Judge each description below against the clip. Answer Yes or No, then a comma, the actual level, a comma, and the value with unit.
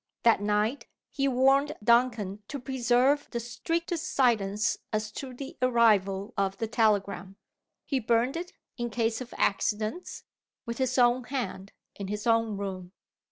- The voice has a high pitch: Yes, high, 235 Hz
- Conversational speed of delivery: Yes, average, 145 wpm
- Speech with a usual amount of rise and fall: Yes, average, 3.7 semitones